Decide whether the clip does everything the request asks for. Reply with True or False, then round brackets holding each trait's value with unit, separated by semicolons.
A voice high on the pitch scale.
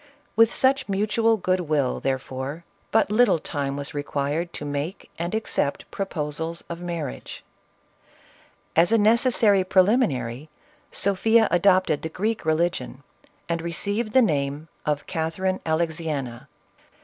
False (170 Hz)